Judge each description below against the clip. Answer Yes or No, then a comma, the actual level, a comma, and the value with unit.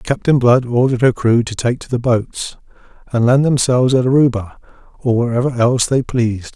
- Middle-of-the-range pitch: No, low, 125 Hz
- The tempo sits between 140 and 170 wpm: No, average, 185 wpm